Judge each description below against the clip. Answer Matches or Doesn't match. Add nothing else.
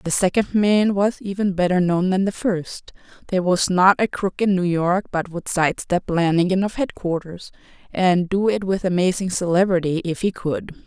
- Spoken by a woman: Matches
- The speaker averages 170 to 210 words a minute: Matches